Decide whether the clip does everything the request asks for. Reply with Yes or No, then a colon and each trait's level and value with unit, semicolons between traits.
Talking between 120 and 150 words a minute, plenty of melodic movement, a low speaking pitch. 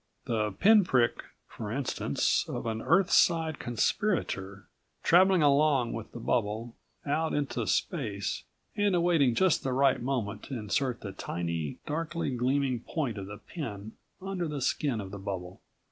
Yes: average, 145 wpm; wide, 6.9 semitones; low, 130 Hz